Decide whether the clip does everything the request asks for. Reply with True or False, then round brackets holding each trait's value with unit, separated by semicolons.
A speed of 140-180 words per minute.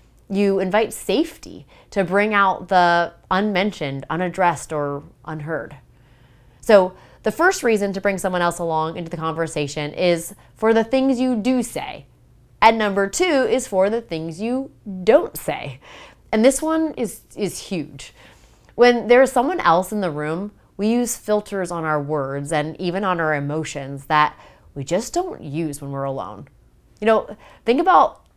True (165 wpm)